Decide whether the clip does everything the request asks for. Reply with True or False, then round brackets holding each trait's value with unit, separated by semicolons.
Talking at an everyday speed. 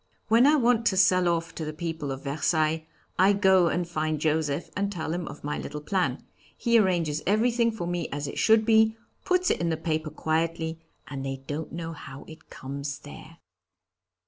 True (195 wpm)